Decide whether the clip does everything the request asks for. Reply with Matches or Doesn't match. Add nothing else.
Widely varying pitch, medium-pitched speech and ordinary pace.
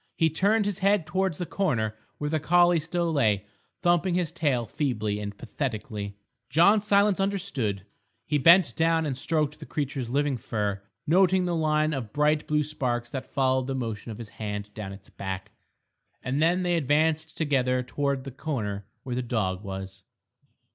Matches